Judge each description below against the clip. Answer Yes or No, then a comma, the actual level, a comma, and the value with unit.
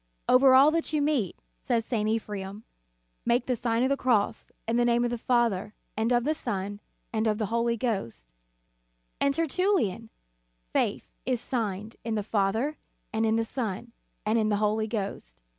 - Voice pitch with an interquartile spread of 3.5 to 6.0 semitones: No, average, 2.9 semitones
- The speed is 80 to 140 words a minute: No, average, 180 wpm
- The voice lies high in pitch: Yes, high, 225 Hz